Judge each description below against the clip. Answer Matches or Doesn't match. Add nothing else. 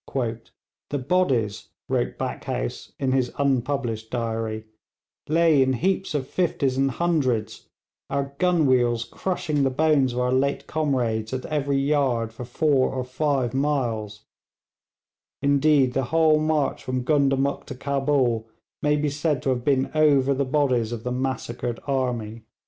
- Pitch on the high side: Doesn't match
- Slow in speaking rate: Doesn't match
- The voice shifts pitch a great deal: Doesn't match